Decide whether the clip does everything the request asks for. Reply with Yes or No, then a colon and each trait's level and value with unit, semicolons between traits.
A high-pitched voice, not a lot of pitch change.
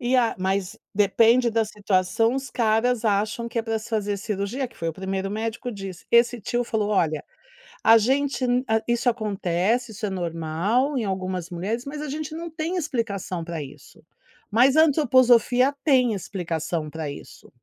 No: high, 220 Hz; average, 4.5 semitones